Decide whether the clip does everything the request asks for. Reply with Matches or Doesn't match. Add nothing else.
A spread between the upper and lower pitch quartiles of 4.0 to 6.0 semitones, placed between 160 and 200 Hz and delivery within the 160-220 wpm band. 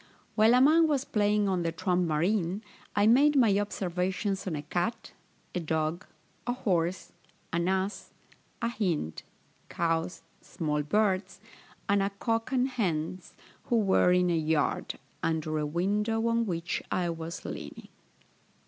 Doesn't match